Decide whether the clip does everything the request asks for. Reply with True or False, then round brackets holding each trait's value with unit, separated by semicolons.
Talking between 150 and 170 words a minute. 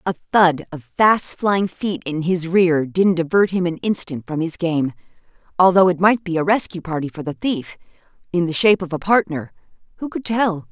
False (195 wpm)